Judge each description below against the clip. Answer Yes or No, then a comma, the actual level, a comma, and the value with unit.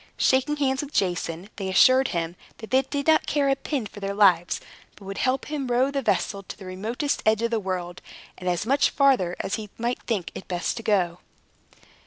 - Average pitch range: No, wide, 6.3 semitones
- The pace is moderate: No, fast, 210 wpm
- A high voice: Yes, high, 220 Hz